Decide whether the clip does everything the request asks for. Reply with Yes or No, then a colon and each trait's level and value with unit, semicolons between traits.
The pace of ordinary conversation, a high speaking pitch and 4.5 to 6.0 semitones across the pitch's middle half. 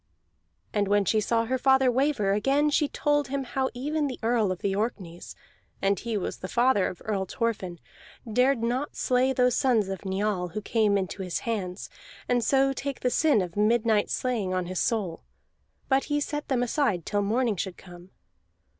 Yes: average, 180 wpm; high, 230 Hz; average, 5.0 semitones